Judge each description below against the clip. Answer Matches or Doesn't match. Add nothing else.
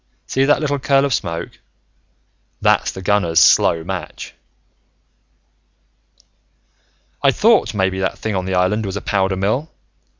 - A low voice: Matches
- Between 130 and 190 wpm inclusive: Matches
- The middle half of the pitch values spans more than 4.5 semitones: Matches